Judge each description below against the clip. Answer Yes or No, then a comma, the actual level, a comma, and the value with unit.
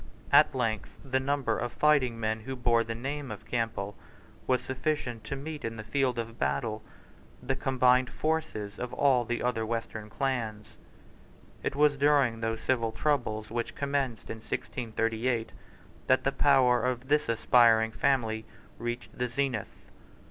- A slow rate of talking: No, average, 150 wpm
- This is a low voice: Yes, low, 120 Hz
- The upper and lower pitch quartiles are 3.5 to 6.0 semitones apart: No, average, 3.0 semitones